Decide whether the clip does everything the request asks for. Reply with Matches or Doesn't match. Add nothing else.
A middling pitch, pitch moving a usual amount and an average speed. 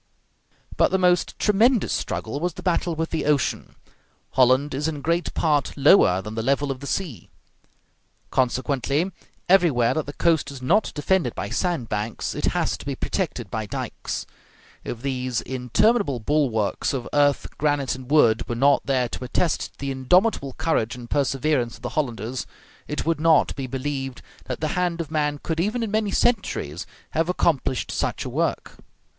Matches